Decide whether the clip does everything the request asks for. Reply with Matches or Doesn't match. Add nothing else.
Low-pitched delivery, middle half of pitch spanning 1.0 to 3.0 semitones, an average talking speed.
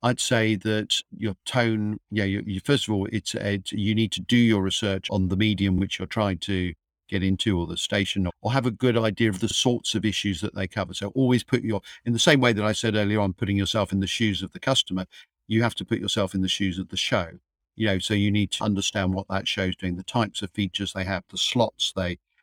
Doesn't match